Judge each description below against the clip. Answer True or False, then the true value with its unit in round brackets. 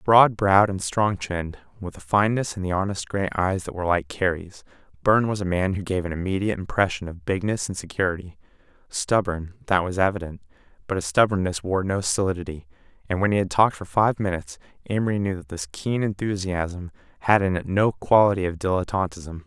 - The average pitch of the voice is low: True (95 Hz)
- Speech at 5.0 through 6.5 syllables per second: True (5.9 syllables/s)